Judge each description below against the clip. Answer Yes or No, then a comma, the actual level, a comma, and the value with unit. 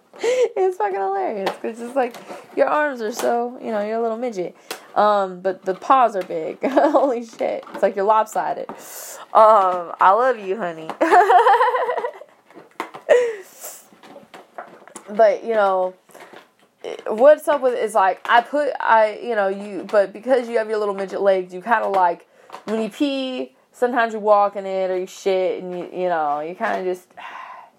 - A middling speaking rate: Yes, average, 175 wpm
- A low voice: No, high, 220 Hz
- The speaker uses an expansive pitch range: Yes, wide, 7.3 semitones